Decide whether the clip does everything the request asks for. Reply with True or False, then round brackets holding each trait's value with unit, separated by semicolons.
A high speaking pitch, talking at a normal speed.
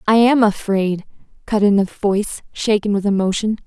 True (205 Hz; 165 wpm)